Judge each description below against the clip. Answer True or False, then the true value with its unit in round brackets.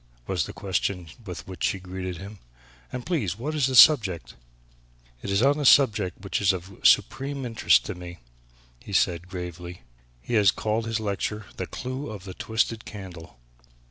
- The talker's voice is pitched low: True (100 Hz)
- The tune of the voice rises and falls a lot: False (4.4 semitones)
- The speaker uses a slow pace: False (175 wpm)